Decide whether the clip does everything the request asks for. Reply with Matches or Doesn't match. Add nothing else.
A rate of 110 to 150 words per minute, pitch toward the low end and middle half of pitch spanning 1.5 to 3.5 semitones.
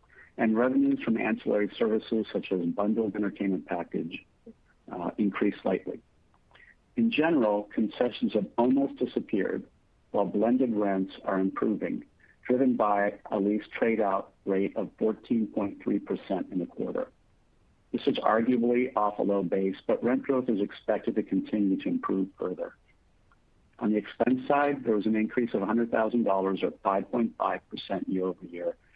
Doesn't match